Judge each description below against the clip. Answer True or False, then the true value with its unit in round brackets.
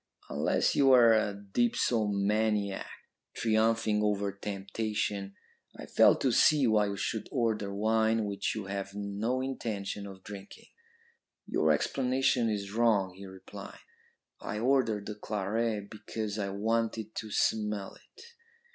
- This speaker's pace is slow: True (130 wpm)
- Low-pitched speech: True (105 Hz)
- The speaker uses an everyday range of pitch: False (2.1 semitones)